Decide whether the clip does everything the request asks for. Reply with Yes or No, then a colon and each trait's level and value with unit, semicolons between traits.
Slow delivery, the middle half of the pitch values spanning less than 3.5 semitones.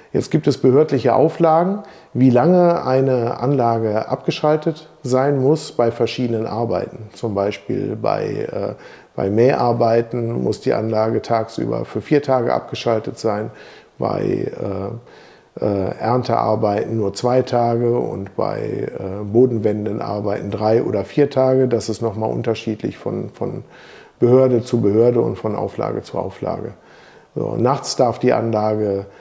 Yes: slow, 130 wpm; average, 3.1 semitones